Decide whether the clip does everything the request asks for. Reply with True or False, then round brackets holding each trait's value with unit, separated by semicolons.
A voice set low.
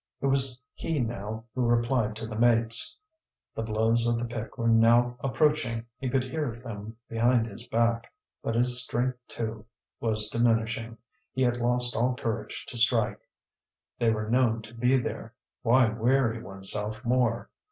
True (115 Hz)